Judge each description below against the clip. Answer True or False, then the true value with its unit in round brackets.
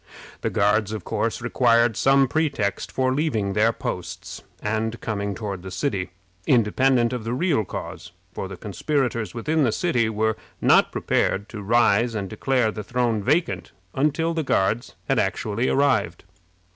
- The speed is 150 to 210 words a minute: True (155 wpm)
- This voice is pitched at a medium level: False (115 Hz)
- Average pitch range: True (4.2 semitones)